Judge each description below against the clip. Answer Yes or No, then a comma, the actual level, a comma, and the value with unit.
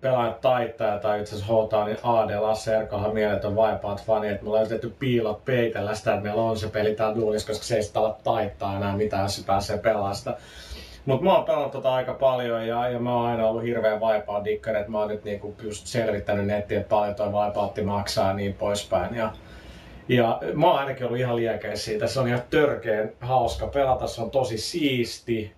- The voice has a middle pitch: No, low, 110 Hz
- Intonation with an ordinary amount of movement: No, narrow, 2.0 semitones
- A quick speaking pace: Yes, fast, 200 wpm